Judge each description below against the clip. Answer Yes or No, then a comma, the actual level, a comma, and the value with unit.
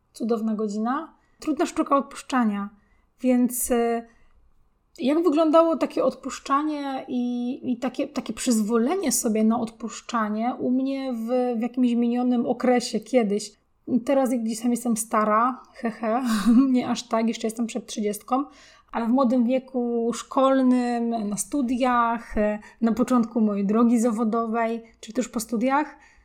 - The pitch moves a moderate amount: No, narrow, 2.1 semitones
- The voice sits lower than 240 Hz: No, high, 245 Hz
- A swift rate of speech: No, average, 130 wpm